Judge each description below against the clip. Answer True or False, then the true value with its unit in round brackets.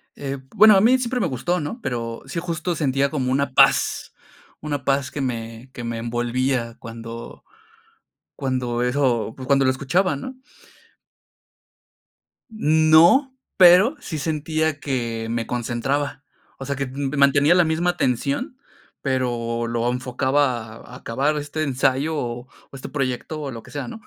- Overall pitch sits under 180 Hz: True (135 Hz)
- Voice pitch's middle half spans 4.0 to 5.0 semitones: True (4.3 semitones)